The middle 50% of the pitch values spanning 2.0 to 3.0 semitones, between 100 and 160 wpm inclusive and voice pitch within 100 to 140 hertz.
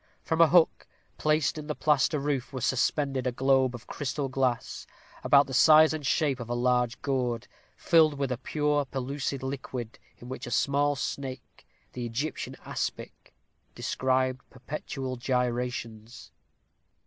Yes: narrow, 2.6 semitones; average, 145 wpm; low, 135 Hz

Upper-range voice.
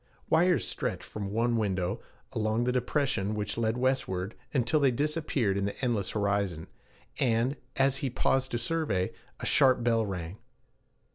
No: low, 115 Hz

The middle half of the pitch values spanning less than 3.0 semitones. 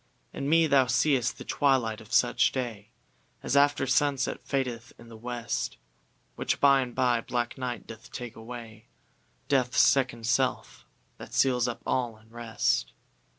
Yes: narrow, 2.5 semitones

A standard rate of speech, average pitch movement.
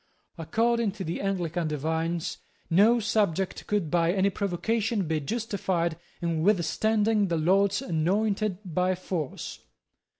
No: slow, 120 wpm; average, 3.9 semitones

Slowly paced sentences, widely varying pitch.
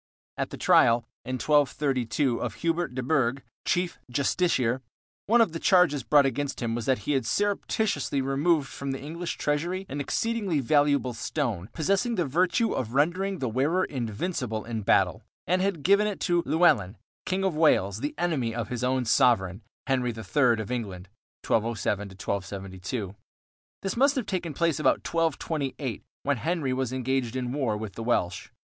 No: average, 165 wpm; wide, 6.3 semitones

